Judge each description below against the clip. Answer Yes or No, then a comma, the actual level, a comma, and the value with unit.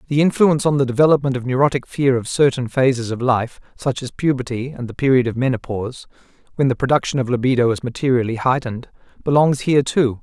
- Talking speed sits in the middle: Yes, average, 190 wpm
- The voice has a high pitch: No, low, 130 Hz